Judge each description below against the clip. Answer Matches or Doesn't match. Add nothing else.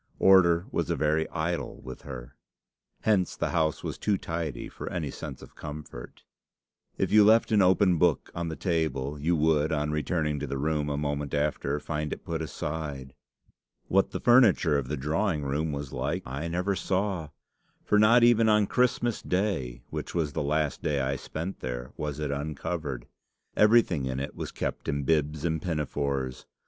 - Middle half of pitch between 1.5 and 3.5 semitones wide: Doesn't match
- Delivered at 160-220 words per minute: Matches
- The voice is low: Matches